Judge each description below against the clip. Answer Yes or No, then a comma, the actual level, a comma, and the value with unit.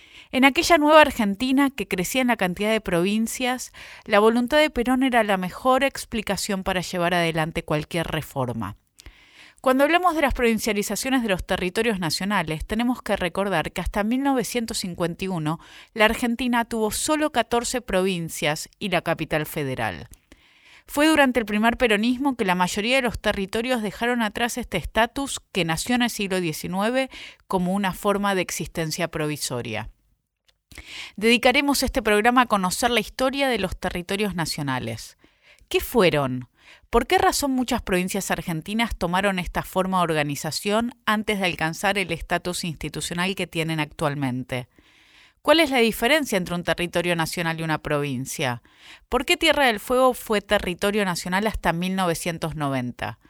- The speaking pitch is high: Yes, high, 200 Hz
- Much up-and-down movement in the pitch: Yes, wide, 6.2 semitones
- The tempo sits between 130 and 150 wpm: Yes, average, 145 wpm